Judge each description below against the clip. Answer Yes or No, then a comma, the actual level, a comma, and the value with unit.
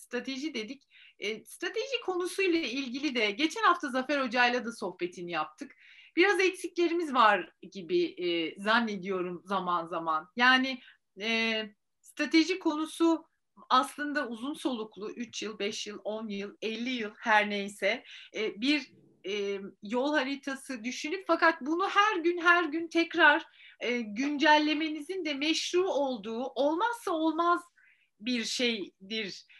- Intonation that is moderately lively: No, wide, 7.4 semitones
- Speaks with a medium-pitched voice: No, very high, 265 Hz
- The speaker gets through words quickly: No, average, 125 wpm